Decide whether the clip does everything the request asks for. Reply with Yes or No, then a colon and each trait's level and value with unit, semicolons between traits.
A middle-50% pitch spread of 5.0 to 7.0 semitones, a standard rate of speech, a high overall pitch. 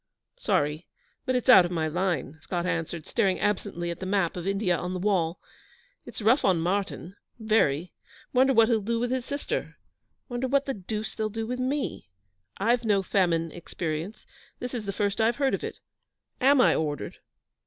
Yes: average, 5.3 semitones; average, 185 wpm; high, 200 Hz